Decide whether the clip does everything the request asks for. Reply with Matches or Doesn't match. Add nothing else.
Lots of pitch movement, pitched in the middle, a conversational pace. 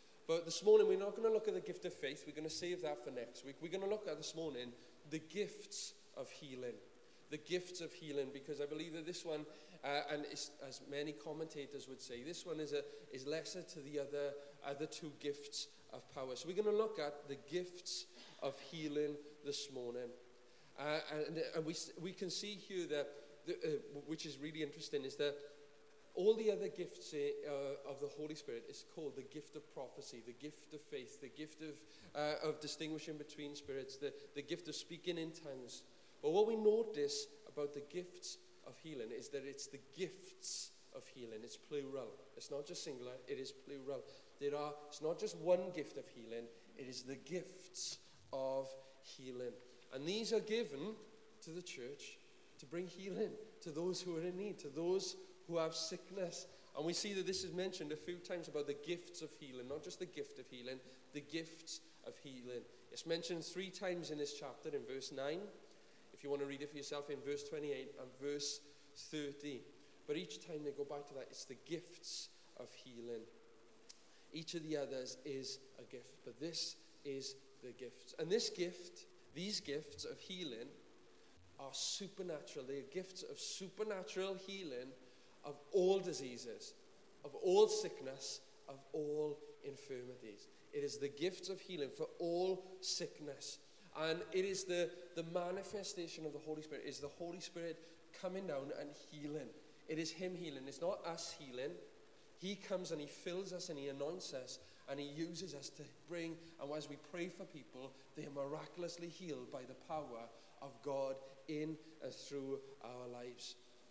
Doesn't match